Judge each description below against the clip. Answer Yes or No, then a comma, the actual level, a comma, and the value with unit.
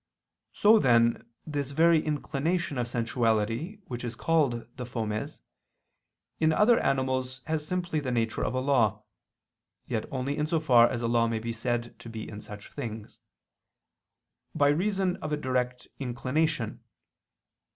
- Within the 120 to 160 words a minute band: Yes, average, 150 wpm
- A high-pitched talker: No, low, 130 Hz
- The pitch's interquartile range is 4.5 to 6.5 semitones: Yes, average, 4.8 semitones